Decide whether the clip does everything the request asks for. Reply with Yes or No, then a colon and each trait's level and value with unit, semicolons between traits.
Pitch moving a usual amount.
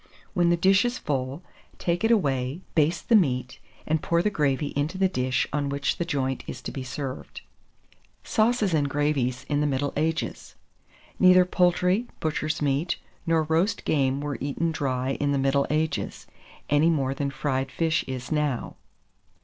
Yes: average, 4.0 semitones